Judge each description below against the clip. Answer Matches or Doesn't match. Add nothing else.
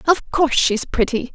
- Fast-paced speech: Doesn't match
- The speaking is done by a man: Doesn't match